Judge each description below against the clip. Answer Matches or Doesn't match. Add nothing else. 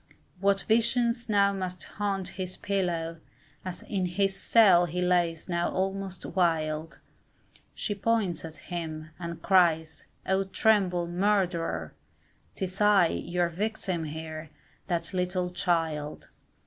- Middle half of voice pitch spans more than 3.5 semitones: Doesn't match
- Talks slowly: Matches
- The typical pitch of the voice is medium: Matches